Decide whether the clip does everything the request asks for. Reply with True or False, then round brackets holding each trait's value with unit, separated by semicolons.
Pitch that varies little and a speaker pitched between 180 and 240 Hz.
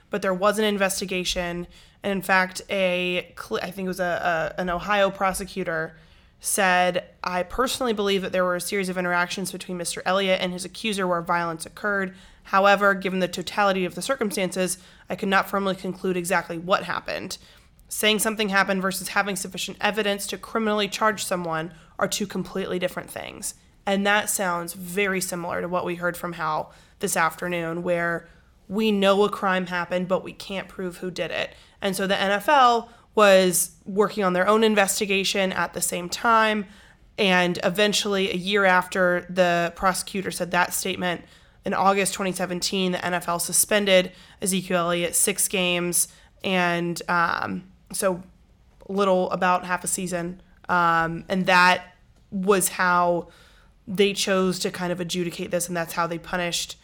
True (2.0 semitones; 185 Hz)